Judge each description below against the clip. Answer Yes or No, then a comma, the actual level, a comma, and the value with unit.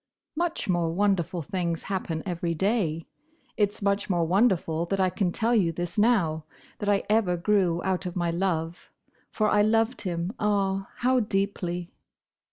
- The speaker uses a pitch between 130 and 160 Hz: No, high, 190 Hz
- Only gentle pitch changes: No, average, 3.3 semitones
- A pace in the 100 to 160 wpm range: Yes, average, 155 wpm